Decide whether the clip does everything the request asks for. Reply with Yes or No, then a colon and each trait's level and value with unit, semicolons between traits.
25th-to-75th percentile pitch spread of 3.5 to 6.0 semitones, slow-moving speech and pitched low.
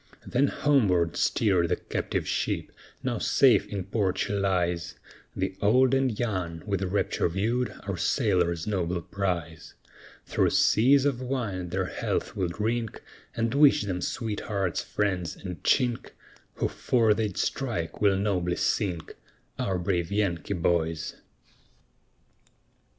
Yes: average, 4.3 semitones; slow, 130 wpm; low, 100 Hz